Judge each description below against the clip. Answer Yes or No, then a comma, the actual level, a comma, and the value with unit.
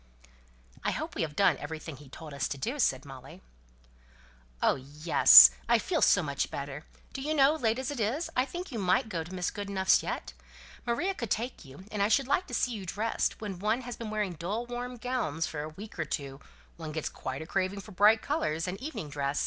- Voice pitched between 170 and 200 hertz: Yes, high, 190 Hz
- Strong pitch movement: Yes, wide, 8.0 semitones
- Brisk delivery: Yes, fast, 225 wpm